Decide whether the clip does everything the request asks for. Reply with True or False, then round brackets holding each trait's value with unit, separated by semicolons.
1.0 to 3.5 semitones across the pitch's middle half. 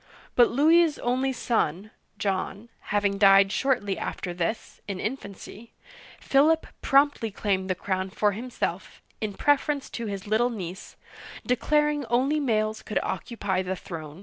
False (5.3 semitones)